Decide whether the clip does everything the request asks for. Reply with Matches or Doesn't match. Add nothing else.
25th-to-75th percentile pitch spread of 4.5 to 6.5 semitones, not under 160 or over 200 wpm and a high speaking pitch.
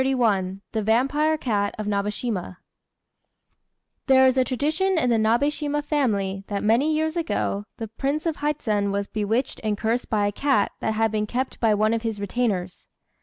Matches